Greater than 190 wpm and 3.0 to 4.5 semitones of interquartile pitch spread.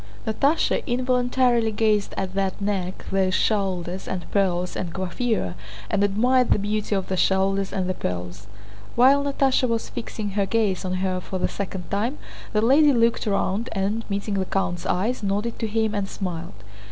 No: average, 170 wpm; average, 3.4 semitones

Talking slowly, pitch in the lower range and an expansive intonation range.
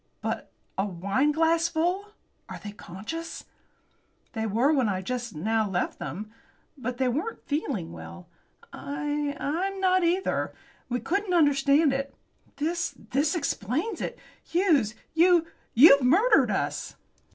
No: slow, 125 wpm; very high, 285 Hz; wide, 6.9 semitones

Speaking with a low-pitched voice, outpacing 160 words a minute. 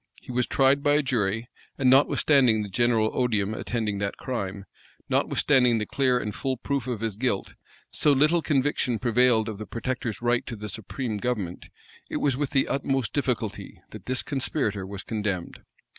Yes: low, 120 Hz; average, 175 wpm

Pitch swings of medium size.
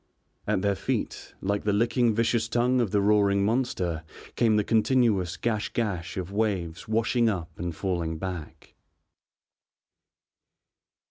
Yes: average, 4.0 semitones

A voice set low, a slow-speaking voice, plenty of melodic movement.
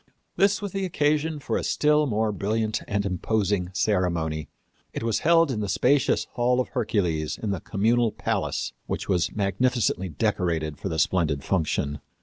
No: low, 105 Hz; average, 160 wpm; wide, 6.0 semitones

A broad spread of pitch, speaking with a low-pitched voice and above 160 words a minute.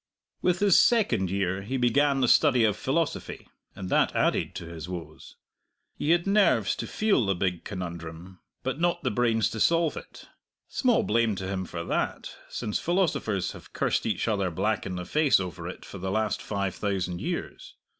Yes: wide, 7.7 semitones; low, 105 Hz; average, 185 wpm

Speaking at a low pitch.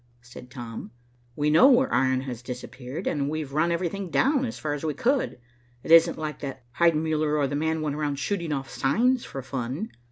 No: medium, 150 Hz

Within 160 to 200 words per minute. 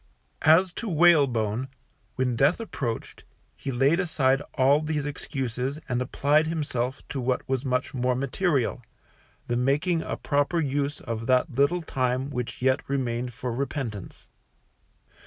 No: average, 140 wpm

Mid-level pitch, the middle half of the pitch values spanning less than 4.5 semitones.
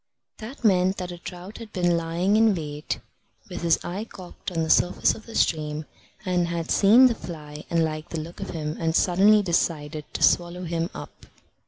Yes: medium, 175 Hz; average, 3.0 semitones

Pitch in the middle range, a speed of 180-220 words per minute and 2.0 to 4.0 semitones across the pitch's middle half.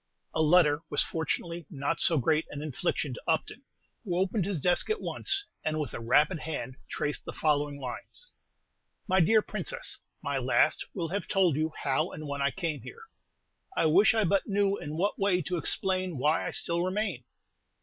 No: medium, 165 Hz; average, 185 wpm; average, 4.5 semitones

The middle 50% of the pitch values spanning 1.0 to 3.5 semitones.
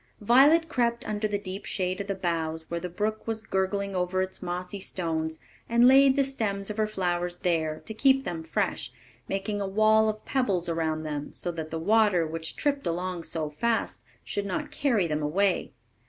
No: average, 4.4 semitones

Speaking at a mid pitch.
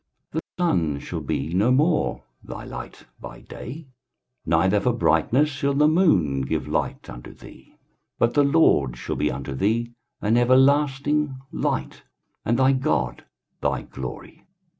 No: low, 120 Hz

